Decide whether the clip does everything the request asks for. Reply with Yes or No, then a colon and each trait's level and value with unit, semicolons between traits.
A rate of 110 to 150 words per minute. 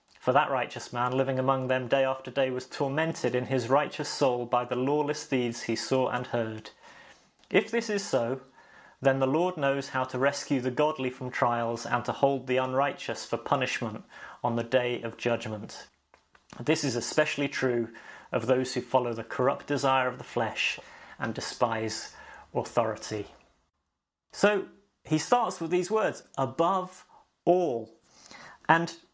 No: average, 160 wpm